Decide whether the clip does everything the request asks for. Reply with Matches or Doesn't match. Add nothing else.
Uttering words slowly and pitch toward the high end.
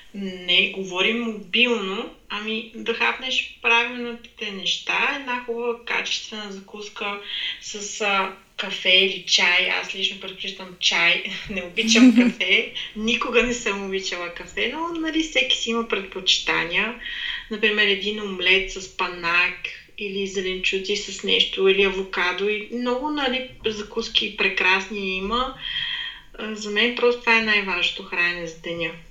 Doesn't match